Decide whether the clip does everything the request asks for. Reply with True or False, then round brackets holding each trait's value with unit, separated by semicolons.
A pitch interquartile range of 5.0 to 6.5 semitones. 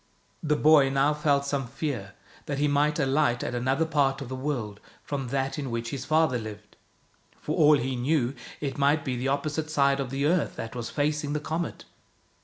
False (2.6 semitones)